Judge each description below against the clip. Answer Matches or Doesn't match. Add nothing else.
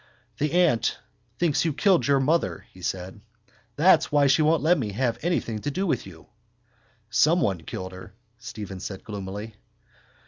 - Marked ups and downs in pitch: Matches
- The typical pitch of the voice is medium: Doesn't match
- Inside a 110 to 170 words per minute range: Matches